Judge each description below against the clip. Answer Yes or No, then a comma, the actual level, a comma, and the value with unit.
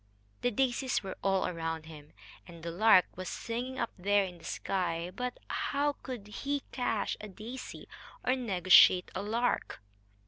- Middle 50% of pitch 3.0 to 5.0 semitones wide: No, wide, 5.6 semitones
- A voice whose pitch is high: Yes, high, 205 Hz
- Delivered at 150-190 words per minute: Yes, average, 160 wpm